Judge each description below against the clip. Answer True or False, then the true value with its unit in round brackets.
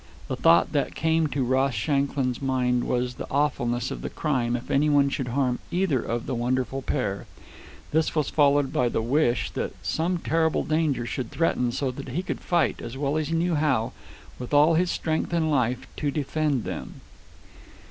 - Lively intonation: False (3.8 semitones)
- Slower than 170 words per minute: False (185 wpm)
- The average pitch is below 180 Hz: True (140 Hz)